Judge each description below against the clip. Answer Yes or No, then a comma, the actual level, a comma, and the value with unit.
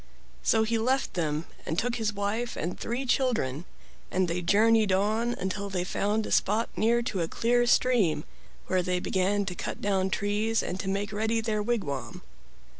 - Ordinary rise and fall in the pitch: Yes, average, 3.5 semitones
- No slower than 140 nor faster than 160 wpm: No, average, 180 wpm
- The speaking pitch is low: No, high, 205 Hz